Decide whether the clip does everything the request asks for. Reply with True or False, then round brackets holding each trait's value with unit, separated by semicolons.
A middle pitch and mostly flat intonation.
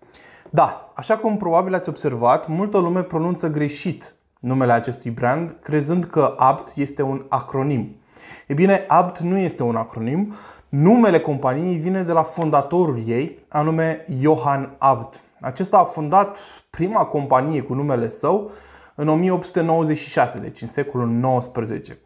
False (155 Hz; 4.7 semitones)